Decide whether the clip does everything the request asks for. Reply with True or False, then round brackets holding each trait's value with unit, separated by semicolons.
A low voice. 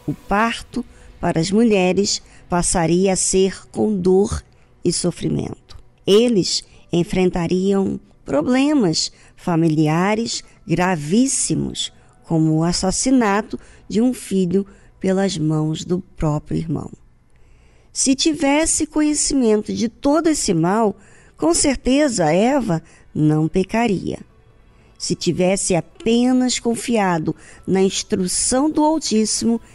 False (190 Hz)